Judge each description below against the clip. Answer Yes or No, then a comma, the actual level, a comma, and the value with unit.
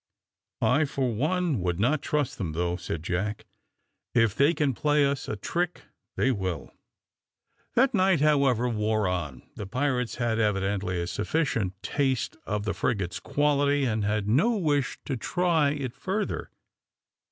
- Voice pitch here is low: Yes, low, 125 Hz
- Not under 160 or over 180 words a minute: No, average, 150 wpm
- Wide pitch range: Yes, wide, 6.7 semitones